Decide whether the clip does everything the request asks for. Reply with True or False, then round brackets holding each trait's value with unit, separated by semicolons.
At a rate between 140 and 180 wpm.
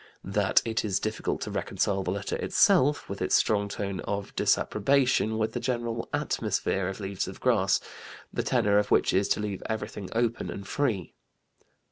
True (170 wpm)